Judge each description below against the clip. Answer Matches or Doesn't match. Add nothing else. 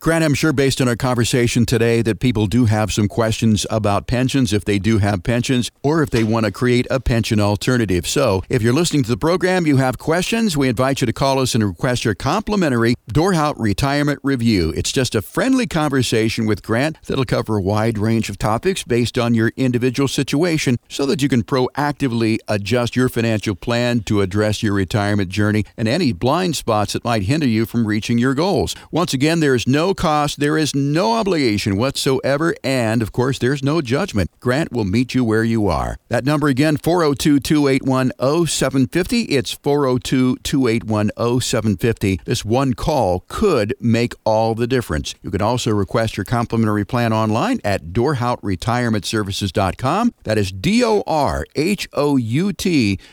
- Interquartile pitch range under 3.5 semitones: Doesn't match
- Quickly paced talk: Doesn't match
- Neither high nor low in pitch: Doesn't match